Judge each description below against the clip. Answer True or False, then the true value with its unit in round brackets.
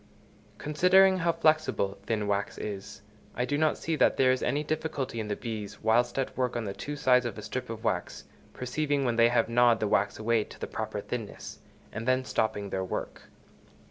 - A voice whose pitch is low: True (120 Hz)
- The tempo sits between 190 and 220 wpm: True (205 wpm)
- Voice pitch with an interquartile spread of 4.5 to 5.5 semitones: True (4.9 semitones)